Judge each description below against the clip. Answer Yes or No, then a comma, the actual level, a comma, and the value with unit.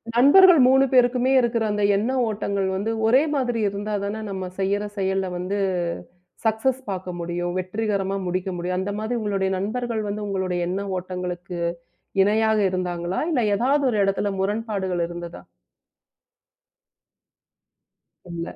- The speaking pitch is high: Yes, high, 200 Hz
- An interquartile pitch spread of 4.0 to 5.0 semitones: No, average, 3.5 semitones